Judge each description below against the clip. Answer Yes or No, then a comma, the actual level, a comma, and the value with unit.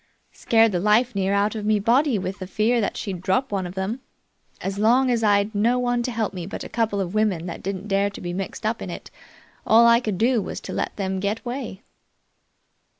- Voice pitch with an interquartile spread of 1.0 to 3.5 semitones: Yes, average, 3.1 semitones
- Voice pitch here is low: No, high, 210 Hz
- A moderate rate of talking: No, fast, 225 wpm